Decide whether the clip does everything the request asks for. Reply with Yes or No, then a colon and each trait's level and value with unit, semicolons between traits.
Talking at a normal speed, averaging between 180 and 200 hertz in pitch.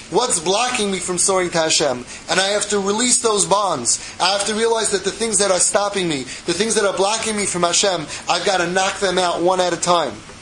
No: fast, 240 wpm; high, 190 Hz